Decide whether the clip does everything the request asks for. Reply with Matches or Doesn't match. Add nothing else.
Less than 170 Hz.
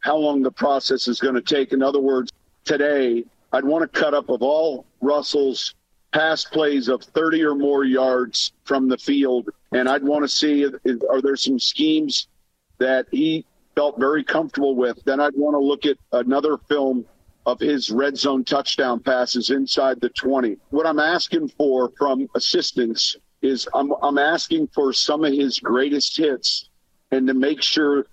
Matches